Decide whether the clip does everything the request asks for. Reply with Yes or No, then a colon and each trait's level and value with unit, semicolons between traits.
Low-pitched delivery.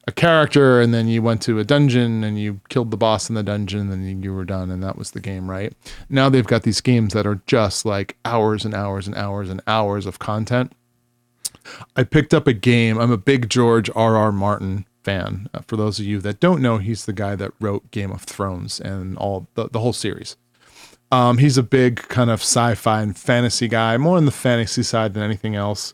Yes: low, 110 Hz